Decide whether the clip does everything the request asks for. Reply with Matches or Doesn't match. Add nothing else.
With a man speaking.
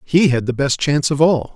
Matches